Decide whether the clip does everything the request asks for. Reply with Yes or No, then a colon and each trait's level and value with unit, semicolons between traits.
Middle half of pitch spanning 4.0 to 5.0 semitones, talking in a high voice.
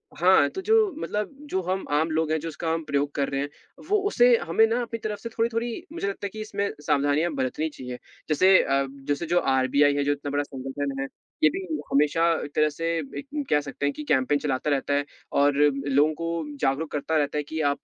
No: average, 4.6 semitones; medium, 150 Hz